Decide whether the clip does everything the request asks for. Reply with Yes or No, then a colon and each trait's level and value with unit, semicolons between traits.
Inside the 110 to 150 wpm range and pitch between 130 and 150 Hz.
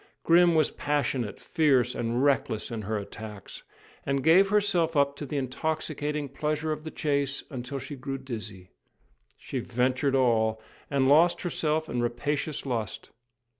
Yes: average, 145 wpm; medium, 140 Hz